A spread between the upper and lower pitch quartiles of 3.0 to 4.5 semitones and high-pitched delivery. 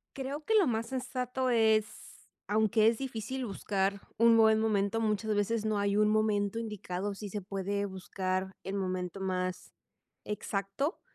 No: narrow, 2.5 semitones; high, 210 Hz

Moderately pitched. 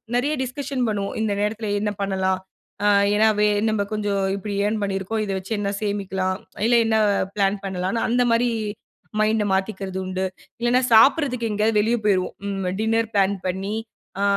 No: high, 210 Hz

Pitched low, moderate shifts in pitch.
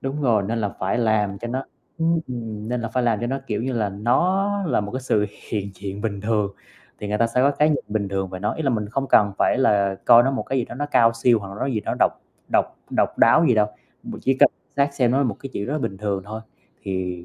Yes: low, 115 Hz; average, 4.4 semitones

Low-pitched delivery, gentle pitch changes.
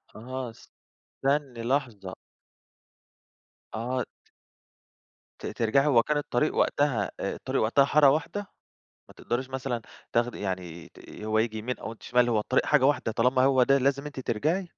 No: low, 125 Hz; average, 3.4 semitones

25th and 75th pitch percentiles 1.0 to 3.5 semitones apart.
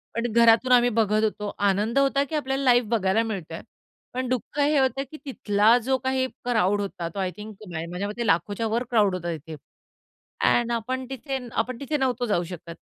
No: average, 4.1 semitones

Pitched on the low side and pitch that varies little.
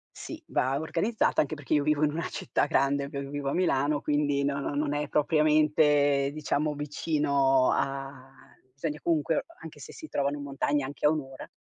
No: medium, 145 Hz; narrow, 1.6 semitones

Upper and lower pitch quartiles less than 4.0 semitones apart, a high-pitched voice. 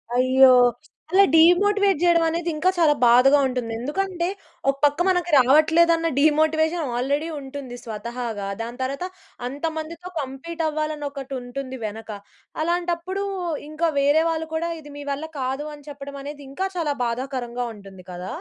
No: average, 4.3 semitones; very high, 290 Hz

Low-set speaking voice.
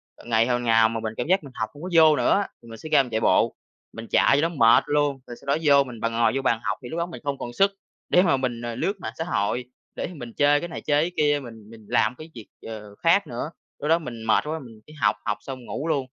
Yes: low, 130 Hz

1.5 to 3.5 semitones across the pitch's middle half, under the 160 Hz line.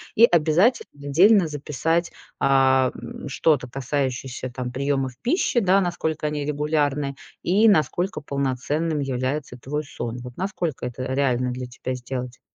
No: average, 4.0 semitones; medium, 140 Hz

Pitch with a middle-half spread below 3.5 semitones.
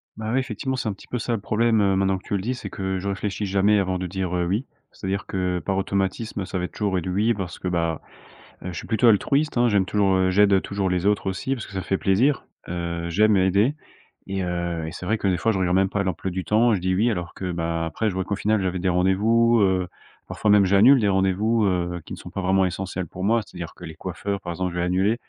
Yes: narrow, 2.6 semitones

